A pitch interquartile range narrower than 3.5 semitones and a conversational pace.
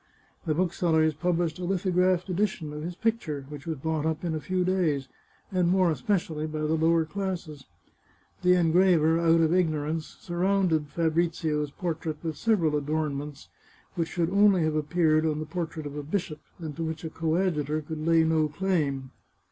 Yes: average, 2.7 semitones; average, 170 wpm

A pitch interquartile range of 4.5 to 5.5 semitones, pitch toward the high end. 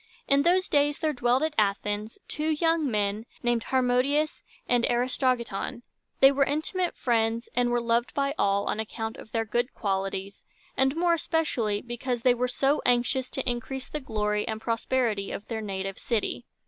No: average, 4.0 semitones; high, 240 Hz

